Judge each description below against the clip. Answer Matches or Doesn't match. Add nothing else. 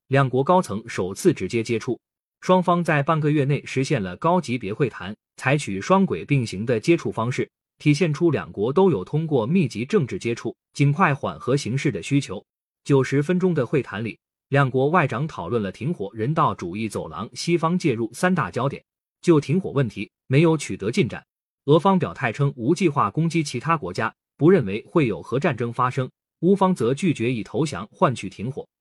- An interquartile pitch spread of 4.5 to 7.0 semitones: Matches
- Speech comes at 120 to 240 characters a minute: Doesn't match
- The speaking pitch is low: Doesn't match